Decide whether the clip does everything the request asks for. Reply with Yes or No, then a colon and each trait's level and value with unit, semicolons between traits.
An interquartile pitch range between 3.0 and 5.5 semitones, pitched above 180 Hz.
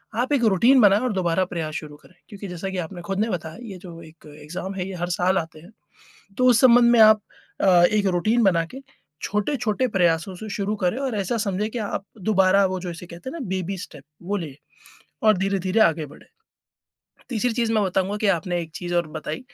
Yes: average, 3.7 semitones; high, 190 Hz